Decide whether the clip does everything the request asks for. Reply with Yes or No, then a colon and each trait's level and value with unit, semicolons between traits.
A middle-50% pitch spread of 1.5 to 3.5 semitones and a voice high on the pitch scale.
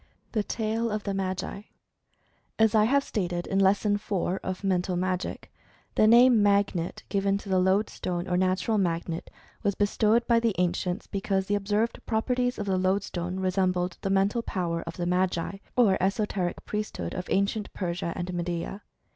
Yes: average, 2.7 semitones; high, 195 Hz